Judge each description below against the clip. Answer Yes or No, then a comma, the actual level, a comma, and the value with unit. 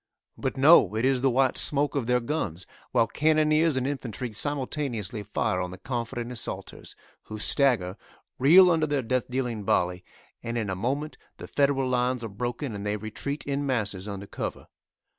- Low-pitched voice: Yes, low, 125 Hz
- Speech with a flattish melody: No, average, 4.6 semitones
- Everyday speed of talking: Yes, average, 175 wpm